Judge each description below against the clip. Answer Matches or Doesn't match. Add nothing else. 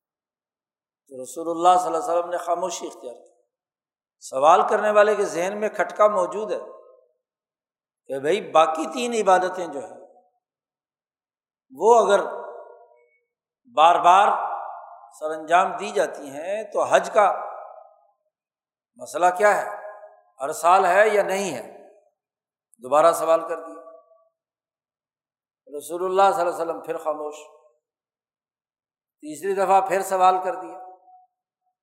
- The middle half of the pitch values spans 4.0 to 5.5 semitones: Matches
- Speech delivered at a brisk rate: Doesn't match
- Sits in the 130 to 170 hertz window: Doesn't match